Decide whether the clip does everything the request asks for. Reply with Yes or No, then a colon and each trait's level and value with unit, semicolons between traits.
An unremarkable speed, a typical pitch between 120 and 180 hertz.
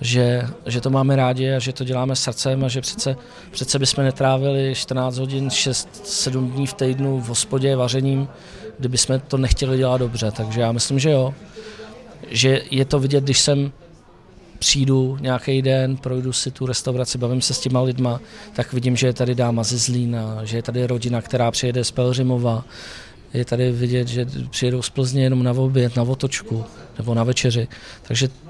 No: fast, 180 wpm; low, 130 Hz